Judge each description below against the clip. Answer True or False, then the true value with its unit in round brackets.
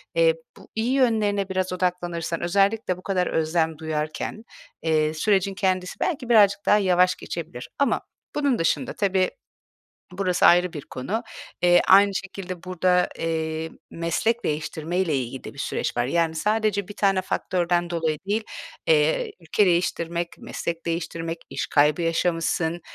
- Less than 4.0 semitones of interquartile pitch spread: True (3.3 semitones)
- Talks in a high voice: False (175 Hz)